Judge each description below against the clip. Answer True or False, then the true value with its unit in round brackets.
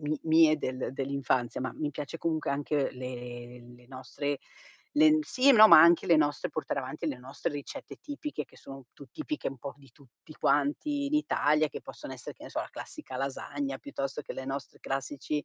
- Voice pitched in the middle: True (145 Hz)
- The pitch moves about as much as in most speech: True (3.3 semitones)